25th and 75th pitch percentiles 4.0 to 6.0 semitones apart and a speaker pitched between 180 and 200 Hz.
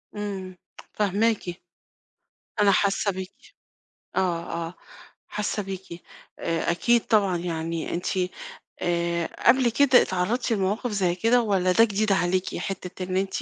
No: average, 2.9 semitones; high, 190 Hz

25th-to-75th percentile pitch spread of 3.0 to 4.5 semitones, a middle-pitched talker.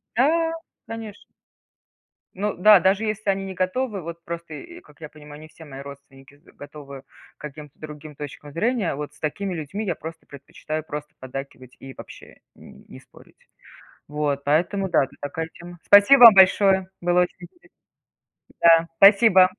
No: average, 5.1 semitones; medium, 170 Hz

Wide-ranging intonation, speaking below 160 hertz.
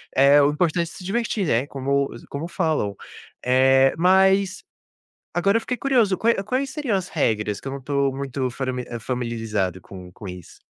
Yes: wide, 7.3 semitones; medium, 140 Hz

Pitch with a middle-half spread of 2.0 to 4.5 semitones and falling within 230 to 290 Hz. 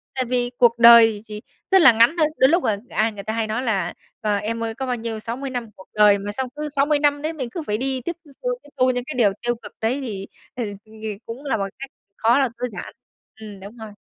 Yes: average, 3.5 semitones; high, 235 Hz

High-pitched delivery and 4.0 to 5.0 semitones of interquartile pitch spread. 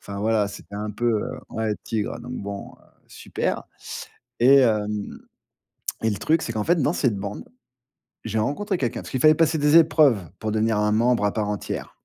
No: low, 110 Hz; average, 4.3 semitones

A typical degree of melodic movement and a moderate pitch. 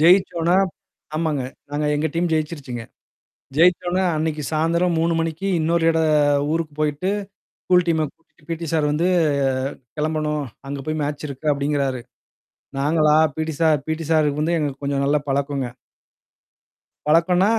No: narrow, 2.1 semitones; medium, 155 Hz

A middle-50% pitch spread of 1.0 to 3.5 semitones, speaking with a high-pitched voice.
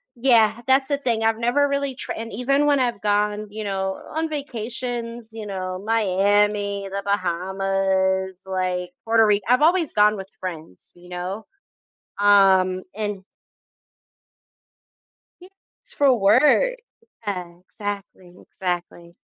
No: average, 4.0 semitones; high, 205 Hz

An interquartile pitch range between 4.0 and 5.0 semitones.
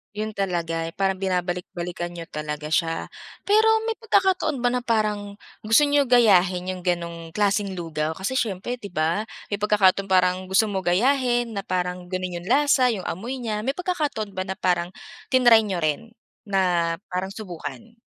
Yes: average, 4.5 semitones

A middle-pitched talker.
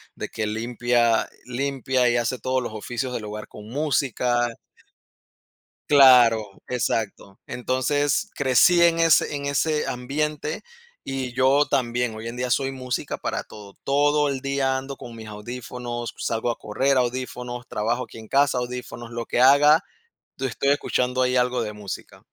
No: low, 125 Hz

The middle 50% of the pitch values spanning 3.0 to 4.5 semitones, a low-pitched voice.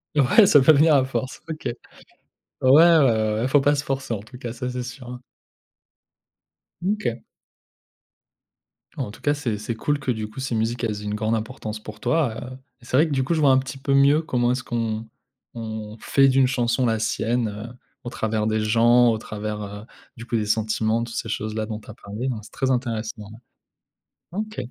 Yes: average, 3.5 semitones; low, 120 Hz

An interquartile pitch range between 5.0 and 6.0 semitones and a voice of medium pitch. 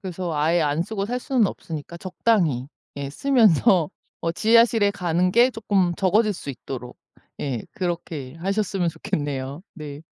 Yes: wide, 5.6 semitones; medium, 175 Hz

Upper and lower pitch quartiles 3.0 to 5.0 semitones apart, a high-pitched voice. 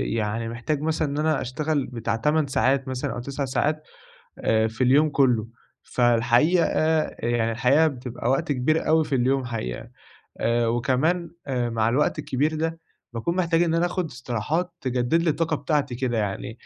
No: average, 4.7 semitones; low, 130 Hz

